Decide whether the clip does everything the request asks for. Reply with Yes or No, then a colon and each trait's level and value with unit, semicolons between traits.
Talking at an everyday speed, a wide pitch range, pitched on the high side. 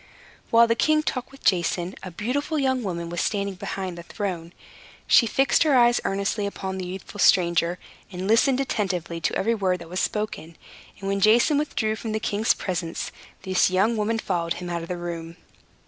No: average, 190 wpm; average, 4.6 semitones; high, 195 Hz